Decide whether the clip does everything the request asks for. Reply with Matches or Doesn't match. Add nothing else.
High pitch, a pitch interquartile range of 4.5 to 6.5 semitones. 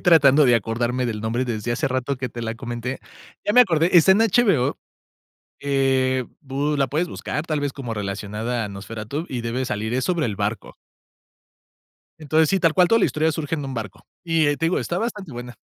Doesn't match